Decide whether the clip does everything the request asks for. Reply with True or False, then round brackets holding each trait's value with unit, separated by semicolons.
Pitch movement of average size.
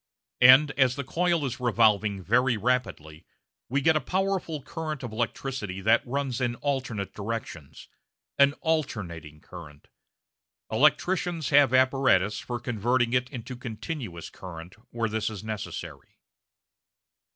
True (4.8 semitones)